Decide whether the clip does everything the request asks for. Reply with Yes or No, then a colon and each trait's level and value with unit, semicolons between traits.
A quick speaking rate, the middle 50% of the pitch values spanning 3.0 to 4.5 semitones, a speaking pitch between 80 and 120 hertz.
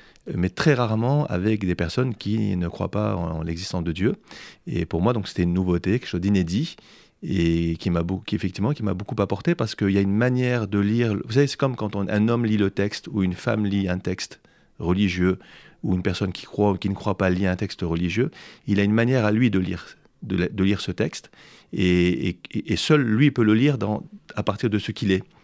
Yes: fast, 245 wpm; average, 3.6 semitones; low, 100 Hz